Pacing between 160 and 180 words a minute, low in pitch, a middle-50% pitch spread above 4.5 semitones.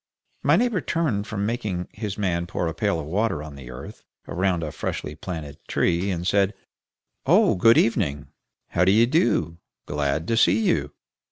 Yes: average, 170 wpm; very low, 95 Hz; wide, 5.6 semitones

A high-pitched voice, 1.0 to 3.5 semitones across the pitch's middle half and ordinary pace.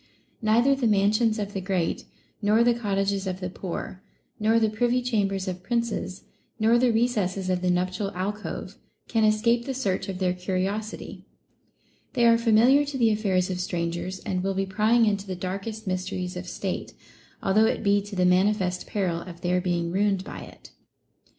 Yes: high, 200 Hz; average, 3.2 semitones; average, 180 wpm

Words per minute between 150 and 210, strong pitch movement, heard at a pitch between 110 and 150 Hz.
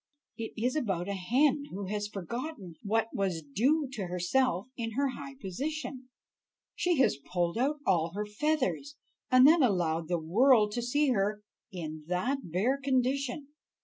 No: average, 155 wpm; wide, 6.8 semitones; high, 225 Hz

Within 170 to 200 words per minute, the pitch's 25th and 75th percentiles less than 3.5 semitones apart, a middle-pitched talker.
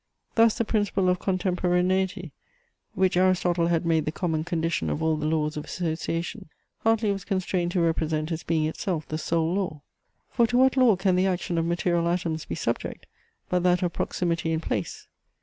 Yes: average, 185 wpm; narrow, 2.6 semitones; medium, 175 Hz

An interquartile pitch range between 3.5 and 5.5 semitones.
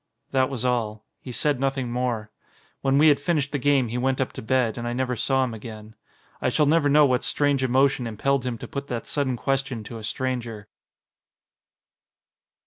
No: average, 2.7 semitones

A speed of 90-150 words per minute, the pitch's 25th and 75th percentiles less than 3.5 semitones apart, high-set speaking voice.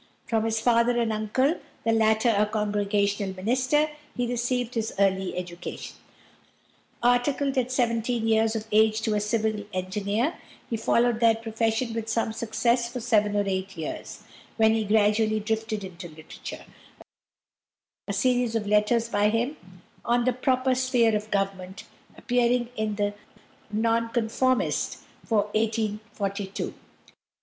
Yes: slow, 135 wpm; narrow, 2.4 semitones; high, 220 Hz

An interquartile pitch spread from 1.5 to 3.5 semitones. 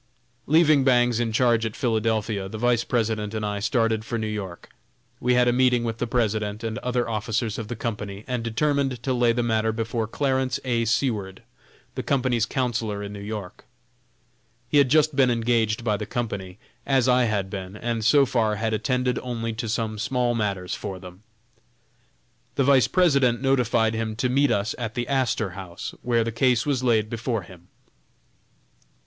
Yes: narrow, 2.6 semitones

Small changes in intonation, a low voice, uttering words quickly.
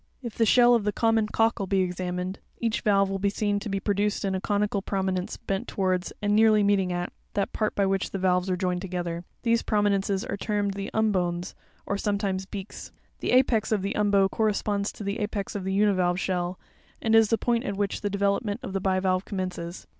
No: narrow, 1.9 semitones; high, 200 Hz; fast, 210 wpm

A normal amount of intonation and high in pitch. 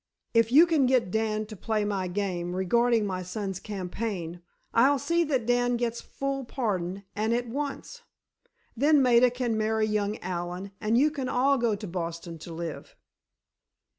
Yes: average, 4.7 semitones; high, 220 Hz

